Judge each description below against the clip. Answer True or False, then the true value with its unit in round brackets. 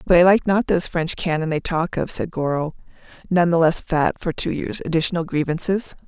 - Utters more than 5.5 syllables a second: False (5.4 syllables/s)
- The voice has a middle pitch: True (170 Hz)